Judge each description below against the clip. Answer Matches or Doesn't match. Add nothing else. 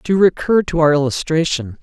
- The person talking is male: Matches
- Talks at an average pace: Matches